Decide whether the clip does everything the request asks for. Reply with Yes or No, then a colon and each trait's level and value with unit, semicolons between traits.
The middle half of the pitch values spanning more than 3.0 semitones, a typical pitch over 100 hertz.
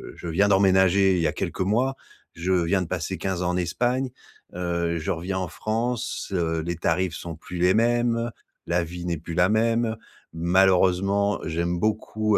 No: average, 3.6 semitones; very low, 95 Hz